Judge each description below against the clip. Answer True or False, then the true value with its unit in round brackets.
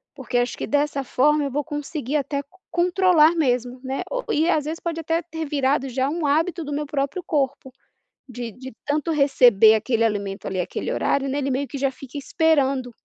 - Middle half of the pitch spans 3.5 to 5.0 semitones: False (3.0 semitones)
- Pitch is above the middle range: True (280 Hz)